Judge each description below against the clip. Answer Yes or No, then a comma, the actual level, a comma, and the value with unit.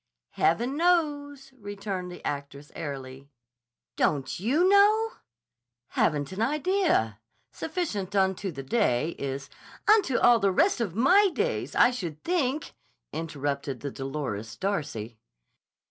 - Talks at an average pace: No, slow, 115 wpm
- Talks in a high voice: Yes, high, 195 Hz